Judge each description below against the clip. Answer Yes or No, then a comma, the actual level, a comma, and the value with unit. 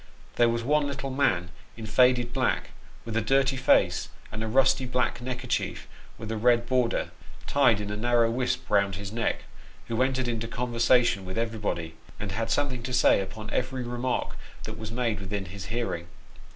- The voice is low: Yes, low, 115 Hz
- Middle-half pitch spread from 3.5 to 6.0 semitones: No, average, 2.9 semitones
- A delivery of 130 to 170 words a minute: No, average, 180 wpm